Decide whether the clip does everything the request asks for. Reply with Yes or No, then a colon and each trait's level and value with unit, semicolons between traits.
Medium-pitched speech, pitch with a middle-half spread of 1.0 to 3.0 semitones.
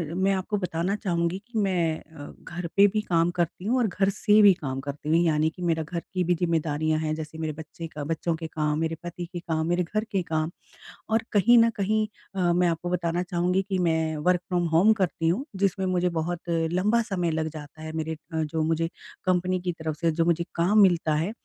Yes: medium, 170 Hz; narrow, 2.5 semitones